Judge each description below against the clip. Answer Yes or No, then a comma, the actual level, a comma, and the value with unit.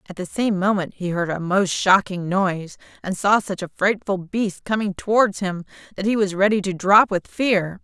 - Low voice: No, high, 195 Hz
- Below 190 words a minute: No, fast, 205 wpm